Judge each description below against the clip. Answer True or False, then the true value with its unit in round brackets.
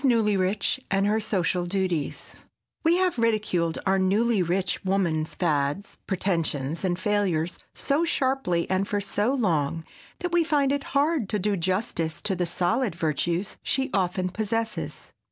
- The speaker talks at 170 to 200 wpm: False (145 wpm)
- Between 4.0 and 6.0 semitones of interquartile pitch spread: True (4.5 semitones)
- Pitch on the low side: False (195 Hz)